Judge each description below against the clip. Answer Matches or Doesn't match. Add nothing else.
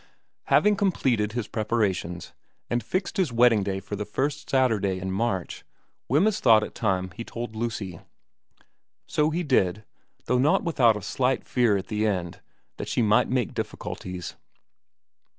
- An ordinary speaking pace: Matches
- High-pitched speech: Doesn't match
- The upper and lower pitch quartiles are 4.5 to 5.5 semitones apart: Matches